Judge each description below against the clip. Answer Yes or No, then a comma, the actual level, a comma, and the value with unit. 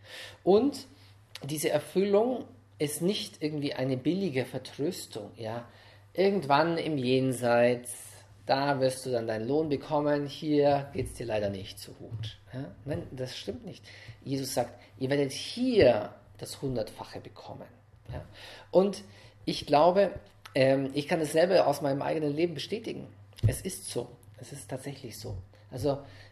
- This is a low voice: Yes, low, 130 Hz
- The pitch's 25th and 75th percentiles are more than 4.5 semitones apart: Yes, average, 5.2 semitones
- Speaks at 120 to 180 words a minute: Yes, average, 140 wpm